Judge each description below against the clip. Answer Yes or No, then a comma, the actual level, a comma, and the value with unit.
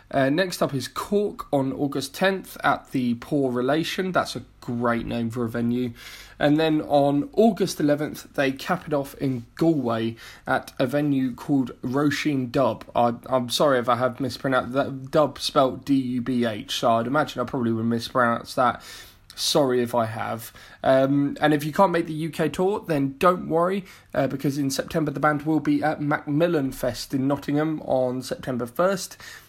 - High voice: No, medium, 140 Hz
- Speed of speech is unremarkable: Yes, average, 175 wpm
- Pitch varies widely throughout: No, average, 3.6 semitones